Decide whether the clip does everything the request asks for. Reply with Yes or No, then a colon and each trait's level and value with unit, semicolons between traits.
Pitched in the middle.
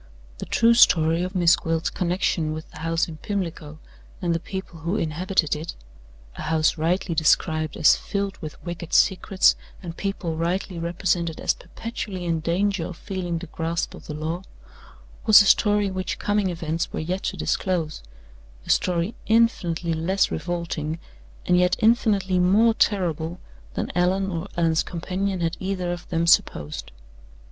Yes: medium, 175 Hz